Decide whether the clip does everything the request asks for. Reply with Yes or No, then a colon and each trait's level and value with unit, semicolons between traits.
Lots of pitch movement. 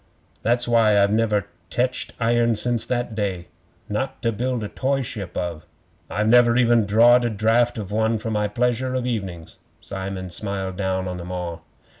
No: average, 3.7 semitones